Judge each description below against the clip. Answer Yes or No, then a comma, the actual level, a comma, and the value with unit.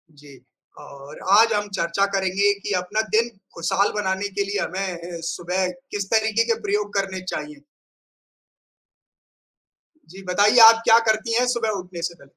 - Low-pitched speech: No, high, 200 Hz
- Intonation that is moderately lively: Yes, average, 3.1 semitones